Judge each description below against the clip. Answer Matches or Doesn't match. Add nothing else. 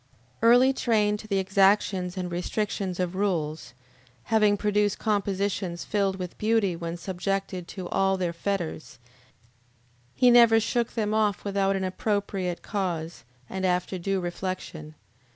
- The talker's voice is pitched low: Doesn't match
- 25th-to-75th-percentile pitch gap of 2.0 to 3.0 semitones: Matches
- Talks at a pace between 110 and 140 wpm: Matches